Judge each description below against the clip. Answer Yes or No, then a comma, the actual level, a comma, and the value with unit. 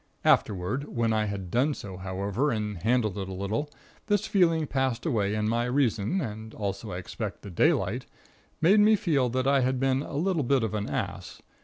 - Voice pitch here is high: No, low, 115 Hz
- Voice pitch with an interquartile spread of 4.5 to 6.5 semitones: Yes, wide, 5.5 semitones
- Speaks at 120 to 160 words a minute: No, average, 195 wpm